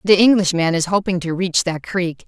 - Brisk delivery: Yes, fast, 210 wpm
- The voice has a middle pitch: Yes, medium, 180 Hz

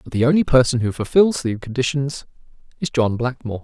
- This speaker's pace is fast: No, average, 180 wpm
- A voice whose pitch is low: Yes, low, 125 Hz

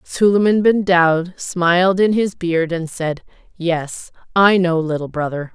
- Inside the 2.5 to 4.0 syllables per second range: Yes, 3.9 syllables/s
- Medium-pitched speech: Yes, medium, 175 Hz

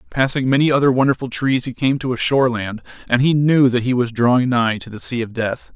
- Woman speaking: No, male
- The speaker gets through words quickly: Yes, fast, 240 wpm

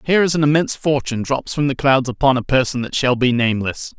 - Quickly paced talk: Yes, fast, 240 wpm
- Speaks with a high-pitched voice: No, low, 135 Hz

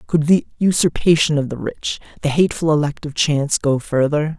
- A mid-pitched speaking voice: Yes, medium, 150 Hz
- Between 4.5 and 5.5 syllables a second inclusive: Yes, 5.4 syllables/s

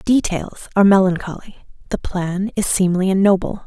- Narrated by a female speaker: Yes, female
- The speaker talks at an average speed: Yes, average, 145 wpm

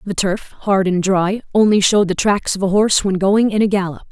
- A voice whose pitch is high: Yes, high, 195 Hz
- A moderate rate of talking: No, fast, 250 wpm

